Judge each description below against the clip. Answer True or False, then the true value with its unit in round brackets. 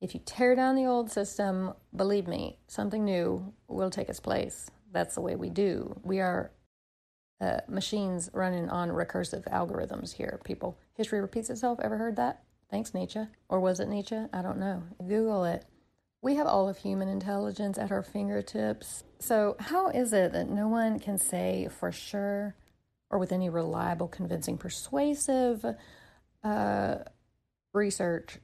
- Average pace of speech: True (160 wpm)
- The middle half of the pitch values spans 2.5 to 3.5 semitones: True (3.0 semitones)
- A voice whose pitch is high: True (200 Hz)